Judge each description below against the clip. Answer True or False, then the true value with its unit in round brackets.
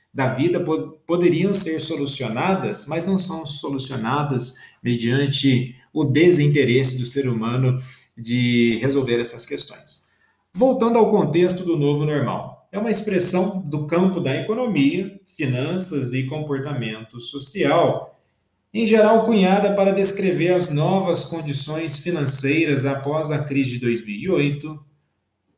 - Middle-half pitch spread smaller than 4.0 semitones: False (5.4 semitones)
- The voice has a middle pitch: True (150 Hz)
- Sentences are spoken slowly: True (115 wpm)